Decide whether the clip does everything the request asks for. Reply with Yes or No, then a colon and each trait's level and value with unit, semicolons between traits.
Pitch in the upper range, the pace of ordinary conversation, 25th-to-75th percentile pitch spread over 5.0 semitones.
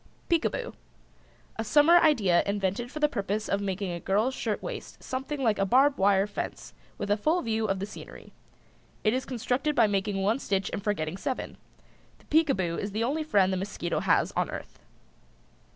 Yes: high, 215 Hz; average, 180 wpm; wide, 5.4 semitones